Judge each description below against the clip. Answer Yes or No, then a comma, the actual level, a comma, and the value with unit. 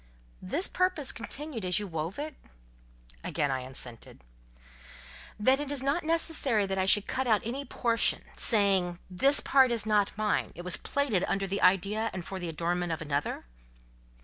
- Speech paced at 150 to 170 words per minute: Yes, average, 165 wpm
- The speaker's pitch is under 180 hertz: No, high, 205 Hz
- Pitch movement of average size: No, wide, 7.0 semitones